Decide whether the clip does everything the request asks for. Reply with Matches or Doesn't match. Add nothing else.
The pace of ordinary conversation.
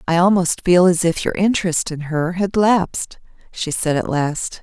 Matches